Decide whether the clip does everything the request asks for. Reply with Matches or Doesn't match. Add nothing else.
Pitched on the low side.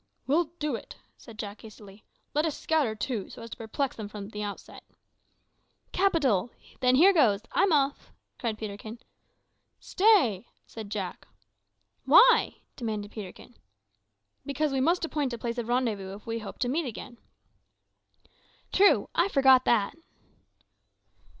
Doesn't match